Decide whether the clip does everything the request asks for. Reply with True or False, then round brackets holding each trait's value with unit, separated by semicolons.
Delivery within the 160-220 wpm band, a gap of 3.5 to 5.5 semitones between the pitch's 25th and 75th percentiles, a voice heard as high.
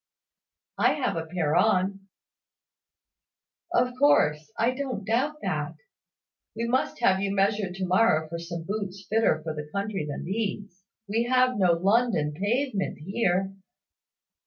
False (135 wpm; 4.5 semitones; 195 Hz)